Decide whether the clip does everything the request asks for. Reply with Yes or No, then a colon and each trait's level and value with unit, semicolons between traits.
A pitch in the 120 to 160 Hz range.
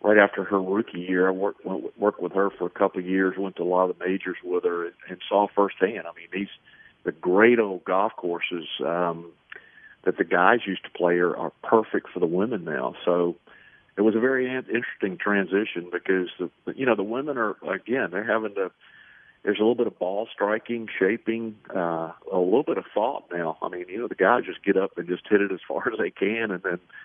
No: very low, 95 Hz